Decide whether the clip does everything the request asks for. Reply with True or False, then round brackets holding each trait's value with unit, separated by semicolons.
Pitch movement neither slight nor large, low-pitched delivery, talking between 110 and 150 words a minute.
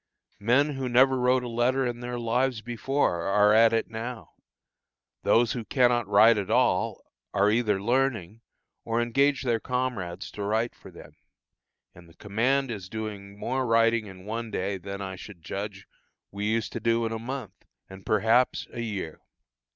False (3.2 semitones; 115 Hz; 170 wpm)